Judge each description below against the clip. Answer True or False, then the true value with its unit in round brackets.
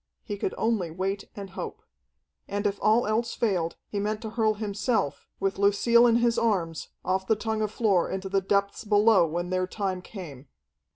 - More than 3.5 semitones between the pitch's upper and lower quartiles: False (2.7 semitones)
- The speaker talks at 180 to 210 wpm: True (185 wpm)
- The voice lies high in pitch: True (200 Hz)